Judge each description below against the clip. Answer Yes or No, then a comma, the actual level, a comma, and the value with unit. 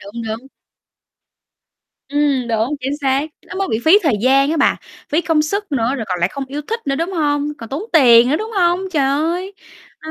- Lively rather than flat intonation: No, average, 4.4 semitones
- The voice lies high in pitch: Yes, very high, 285 Hz